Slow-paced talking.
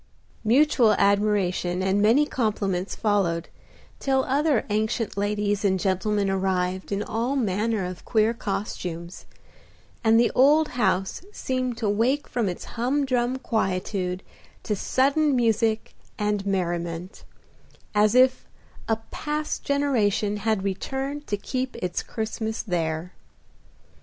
Yes: slow, 115 wpm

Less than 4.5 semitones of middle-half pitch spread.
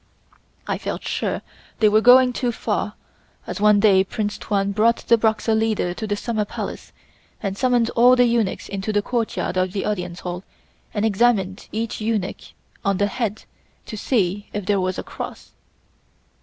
Yes: average, 2.7 semitones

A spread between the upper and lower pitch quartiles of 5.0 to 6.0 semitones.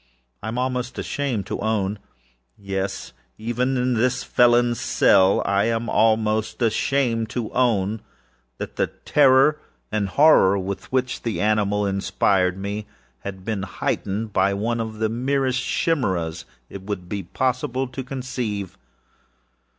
No: average, 4.1 semitones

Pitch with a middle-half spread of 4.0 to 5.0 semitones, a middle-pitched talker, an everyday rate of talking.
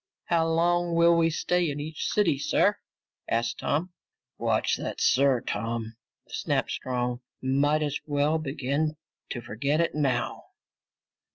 No: average, 4.4 semitones; medium, 145 Hz; slow, 130 wpm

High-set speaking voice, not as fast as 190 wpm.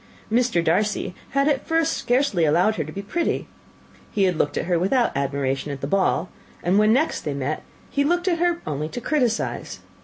No: high, 200 Hz; average, 195 wpm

